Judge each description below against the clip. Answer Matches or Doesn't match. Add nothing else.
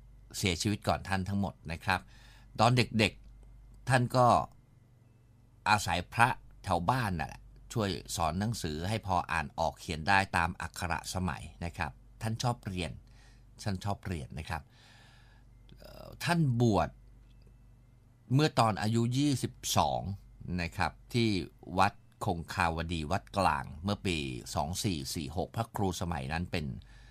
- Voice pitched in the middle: Doesn't match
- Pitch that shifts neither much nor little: Matches